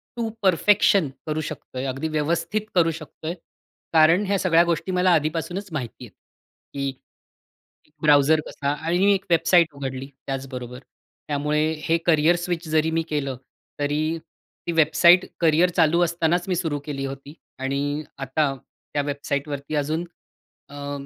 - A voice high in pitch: No, medium, 155 Hz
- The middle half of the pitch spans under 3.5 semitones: Yes, average, 3.1 semitones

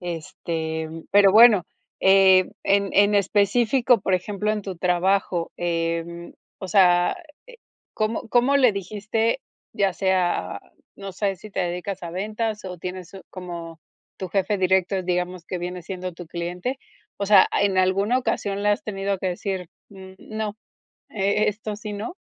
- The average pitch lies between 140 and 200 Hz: Yes, high, 190 Hz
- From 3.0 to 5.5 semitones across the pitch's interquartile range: No, narrow, 2.6 semitones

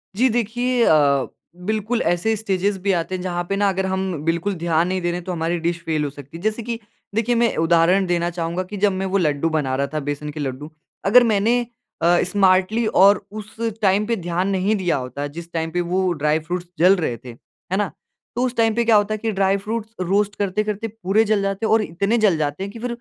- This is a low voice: No, high, 190 Hz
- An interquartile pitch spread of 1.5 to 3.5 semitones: No, average, 4.0 semitones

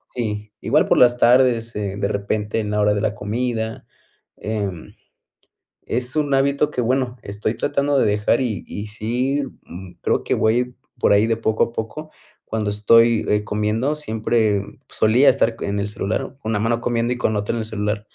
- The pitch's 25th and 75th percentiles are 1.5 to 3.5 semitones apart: Yes, average, 2.8 semitones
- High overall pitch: No, low, 110 Hz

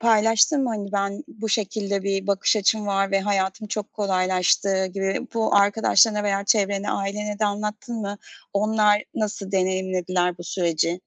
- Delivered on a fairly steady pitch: Yes, narrow, 1.6 semitones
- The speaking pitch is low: No, high, 200 Hz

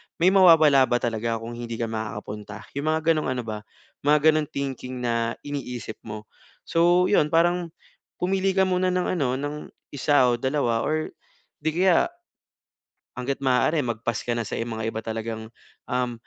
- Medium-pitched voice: No, low, 130 Hz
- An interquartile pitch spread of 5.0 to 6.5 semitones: Yes, wide, 5.5 semitones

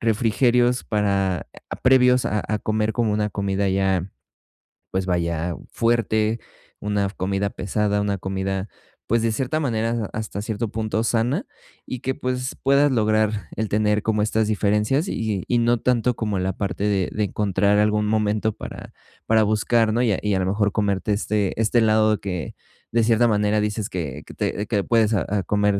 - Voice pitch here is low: Yes, low, 105 Hz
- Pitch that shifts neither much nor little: No, narrow, 2.2 semitones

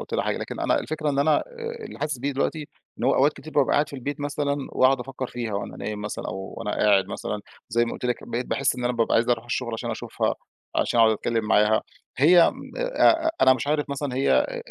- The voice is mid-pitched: No, low, 130 Hz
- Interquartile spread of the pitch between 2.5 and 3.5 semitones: No, average, 4.3 semitones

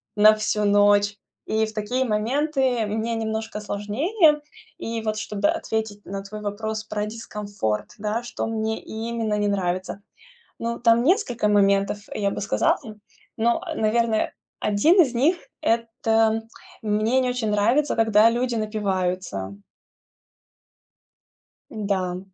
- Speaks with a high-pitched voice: Yes, high, 220 Hz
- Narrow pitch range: Yes, narrow, 2.2 semitones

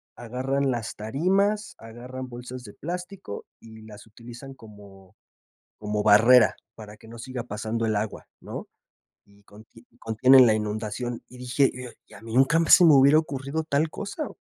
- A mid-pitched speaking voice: No, low, 120 Hz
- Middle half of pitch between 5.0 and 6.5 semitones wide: No, average, 3.9 semitones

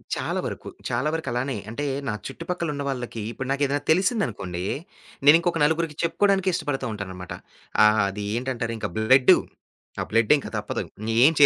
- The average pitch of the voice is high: No, low, 135 Hz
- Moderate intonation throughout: No, wide, 6.0 semitones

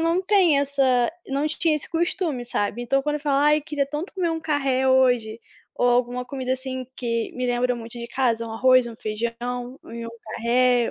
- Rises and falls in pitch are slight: No, average, 3.7 semitones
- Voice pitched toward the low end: No, very high, 255 Hz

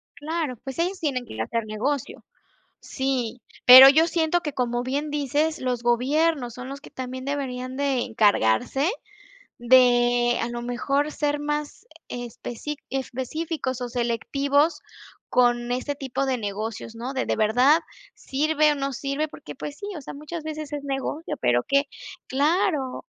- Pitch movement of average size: Yes, average, 3.4 semitones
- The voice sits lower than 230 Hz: No, very high, 270 Hz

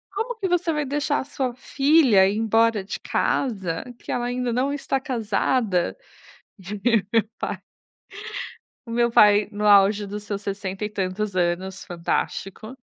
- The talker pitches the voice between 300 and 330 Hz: No, high, 215 Hz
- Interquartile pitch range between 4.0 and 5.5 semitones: Yes, average, 4.8 semitones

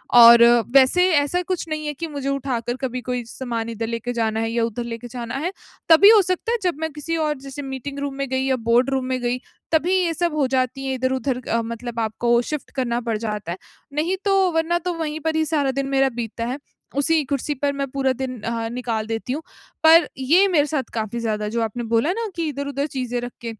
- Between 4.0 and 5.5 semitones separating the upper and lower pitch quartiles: Yes, average, 4.4 semitones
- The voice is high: Yes, very high, 265 Hz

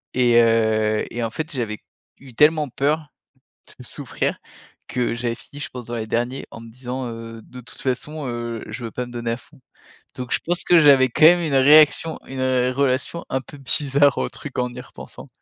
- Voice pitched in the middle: No, low, 125 Hz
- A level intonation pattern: No, average, 3.5 semitones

